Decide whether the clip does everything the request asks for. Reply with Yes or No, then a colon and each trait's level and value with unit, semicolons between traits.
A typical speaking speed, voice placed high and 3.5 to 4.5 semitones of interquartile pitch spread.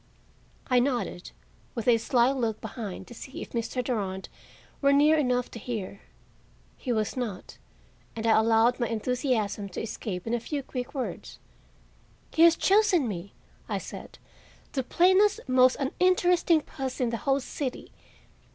Yes: average, 150 wpm; very high, 250 Hz; average, 3.8 semitones